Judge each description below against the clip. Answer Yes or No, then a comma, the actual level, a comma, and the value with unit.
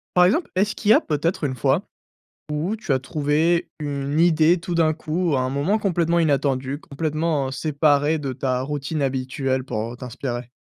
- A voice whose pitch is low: No, medium, 150 Hz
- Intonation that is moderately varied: Yes, average, 3.7 semitones